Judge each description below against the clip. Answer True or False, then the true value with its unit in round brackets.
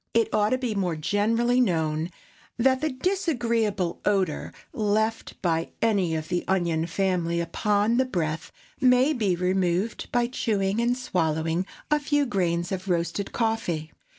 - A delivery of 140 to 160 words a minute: True (145 wpm)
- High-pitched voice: True (200 Hz)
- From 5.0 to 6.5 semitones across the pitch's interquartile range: True (5.6 semitones)